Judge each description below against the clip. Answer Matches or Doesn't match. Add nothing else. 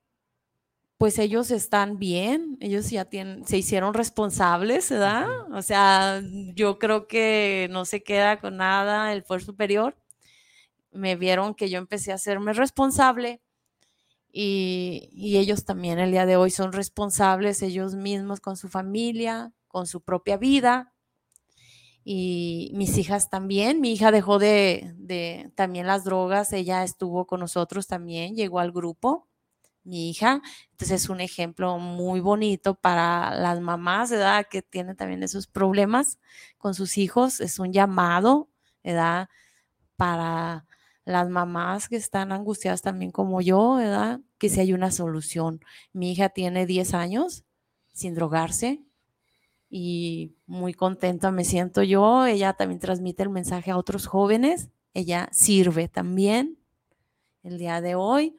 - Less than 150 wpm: Matches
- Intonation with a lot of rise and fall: Doesn't match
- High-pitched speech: Matches